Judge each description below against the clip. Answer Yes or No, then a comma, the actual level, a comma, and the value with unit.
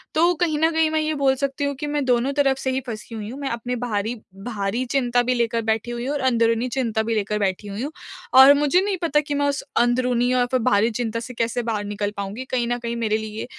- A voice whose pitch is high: Yes, high, 245 Hz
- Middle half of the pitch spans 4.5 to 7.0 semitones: No, average, 3.7 semitones